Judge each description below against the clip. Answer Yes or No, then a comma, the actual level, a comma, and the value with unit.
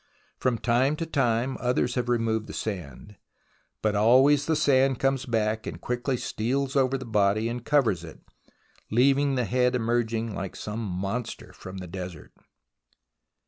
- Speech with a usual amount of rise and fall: Yes, average, 3.5 semitones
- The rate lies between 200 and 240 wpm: No, average, 150 wpm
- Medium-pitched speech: No, low, 120 Hz